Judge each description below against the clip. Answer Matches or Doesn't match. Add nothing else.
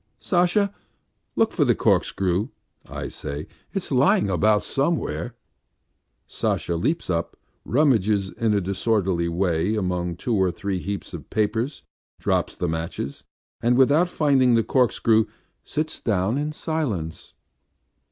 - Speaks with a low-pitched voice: Matches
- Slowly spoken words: Matches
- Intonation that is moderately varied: Doesn't match